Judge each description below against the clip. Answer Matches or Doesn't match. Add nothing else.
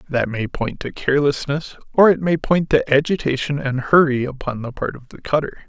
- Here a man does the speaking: Matches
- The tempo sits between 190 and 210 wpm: Matches